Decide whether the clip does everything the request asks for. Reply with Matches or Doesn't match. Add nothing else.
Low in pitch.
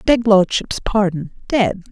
Doesn't match